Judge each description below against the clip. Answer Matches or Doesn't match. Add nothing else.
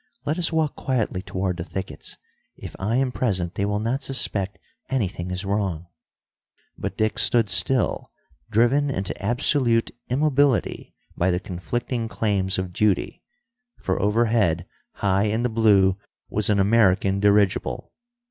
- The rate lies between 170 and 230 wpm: Doesn't match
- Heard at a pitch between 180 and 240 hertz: Doesn't match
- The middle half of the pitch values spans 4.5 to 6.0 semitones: Doesn't match